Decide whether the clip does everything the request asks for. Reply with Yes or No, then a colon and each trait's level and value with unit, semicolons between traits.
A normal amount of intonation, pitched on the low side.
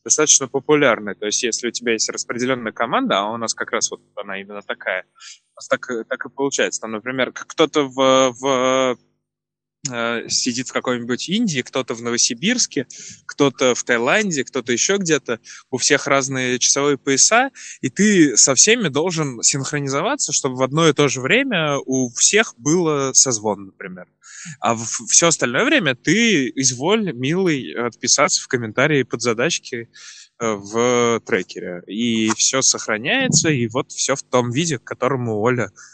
Yes: average, 3.7 semitones; low, 130 Hz